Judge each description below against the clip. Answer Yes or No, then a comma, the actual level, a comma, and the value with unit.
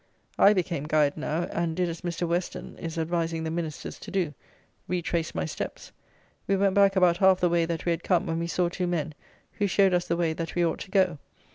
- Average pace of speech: No, fast, 230 wpm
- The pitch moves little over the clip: Yes, narrow, 1.8 semitones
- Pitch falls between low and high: Yes, medium, 170 Hz